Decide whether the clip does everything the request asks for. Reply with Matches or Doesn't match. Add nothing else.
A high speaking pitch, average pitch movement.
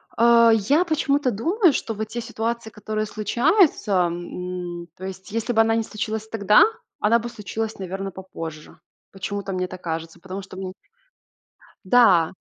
Matches